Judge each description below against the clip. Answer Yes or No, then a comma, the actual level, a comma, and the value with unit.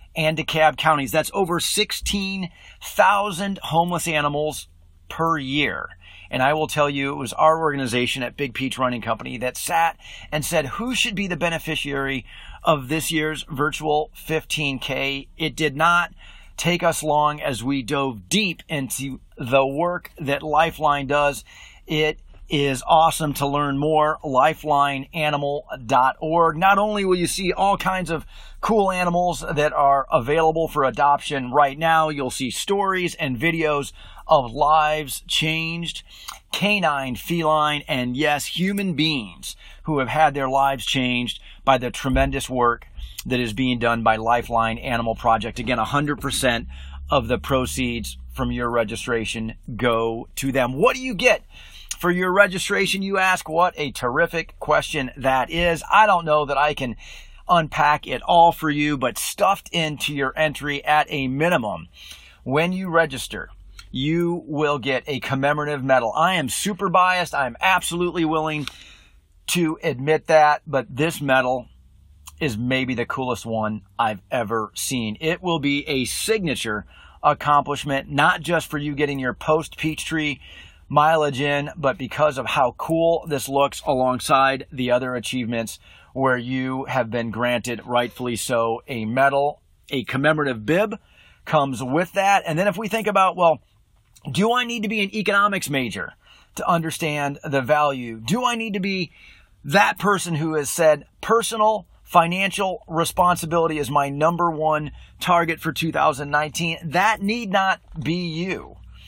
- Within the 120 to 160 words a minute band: Yes, average, 150 wpm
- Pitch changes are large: No, average, 4.3 semitones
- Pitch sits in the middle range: Yes, medium, 150 Hz